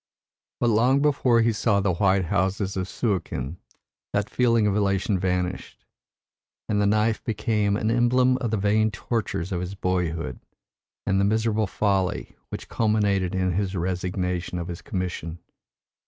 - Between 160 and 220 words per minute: No, average, 150 wpm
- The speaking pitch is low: Yes, low, 100 Hz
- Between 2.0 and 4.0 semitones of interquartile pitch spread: Yes, average, 3.0 semitones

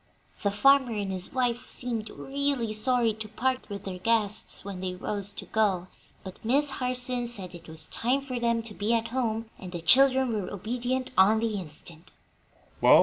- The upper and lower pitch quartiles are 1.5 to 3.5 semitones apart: No, average, 4.0 semitones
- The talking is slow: No, average, 185 wpm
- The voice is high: Yes, high, 225 Hz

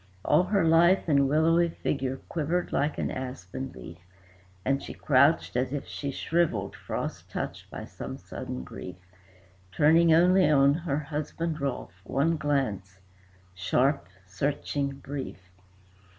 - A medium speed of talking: No, slow, 130 wpm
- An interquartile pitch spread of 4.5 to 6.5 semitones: No, average, 4.0 semitones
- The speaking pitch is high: No, medium, 140 Hz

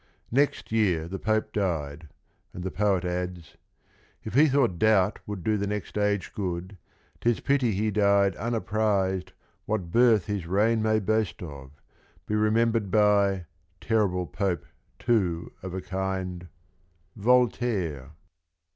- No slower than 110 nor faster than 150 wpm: Yes, average, 140 wpm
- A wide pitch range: No, average, 3.3 semitones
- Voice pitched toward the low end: Yes, low, 100 Hz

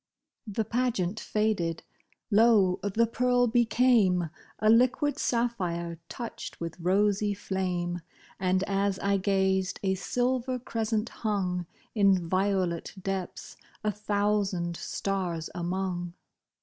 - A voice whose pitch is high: Yes, high, 195 Hz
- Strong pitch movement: No, average, 3.4 semitones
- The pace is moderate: No, slow, 105 wpm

